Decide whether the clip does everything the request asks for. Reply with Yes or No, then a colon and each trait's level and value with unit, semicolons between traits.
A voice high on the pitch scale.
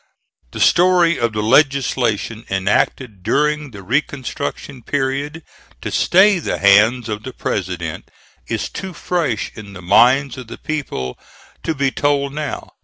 No: low, 130 Hz